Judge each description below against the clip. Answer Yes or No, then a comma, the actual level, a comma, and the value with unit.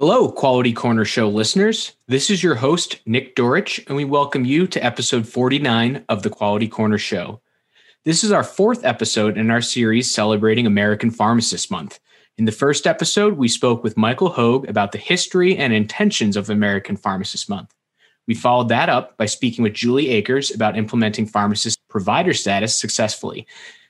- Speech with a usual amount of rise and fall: Yes, average, 4.5 semitones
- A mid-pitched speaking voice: No, low, 120 Hz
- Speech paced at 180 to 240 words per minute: No, average, 170 wpm